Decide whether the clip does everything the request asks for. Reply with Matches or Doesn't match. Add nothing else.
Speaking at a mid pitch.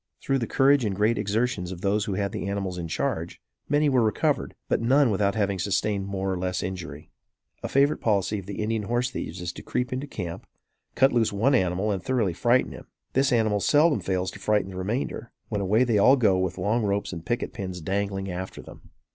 Doesn't match